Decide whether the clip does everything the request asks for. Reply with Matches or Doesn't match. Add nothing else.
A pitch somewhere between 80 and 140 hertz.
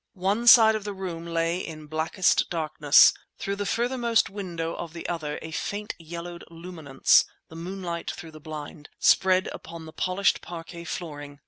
Doesn't match